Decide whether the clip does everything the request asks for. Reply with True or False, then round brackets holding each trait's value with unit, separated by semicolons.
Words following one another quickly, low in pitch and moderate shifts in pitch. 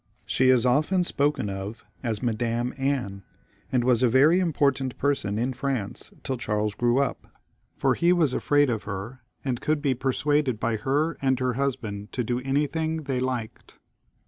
False (170 wpm; 130 Hz; 3.4 semitones)